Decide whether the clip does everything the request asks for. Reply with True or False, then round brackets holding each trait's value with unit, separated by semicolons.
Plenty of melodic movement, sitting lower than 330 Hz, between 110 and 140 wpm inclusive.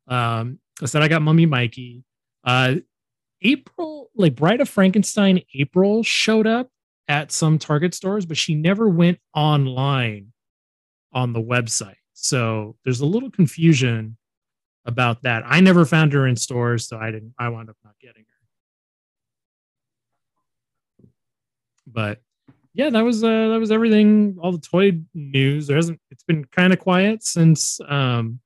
False (7.2 semitones; 140 Hz; 150 wpm)